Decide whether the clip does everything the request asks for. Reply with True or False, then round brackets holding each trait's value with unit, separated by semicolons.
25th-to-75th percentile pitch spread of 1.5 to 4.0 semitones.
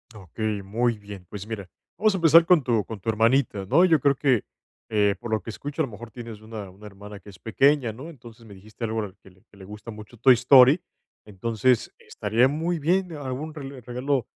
False (4.9 semitones)